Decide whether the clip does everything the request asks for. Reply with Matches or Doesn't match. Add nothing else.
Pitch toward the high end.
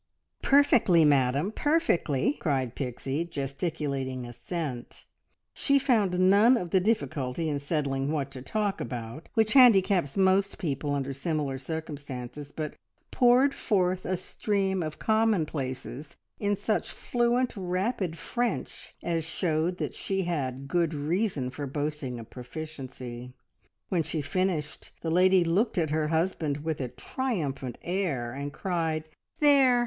Doesn't match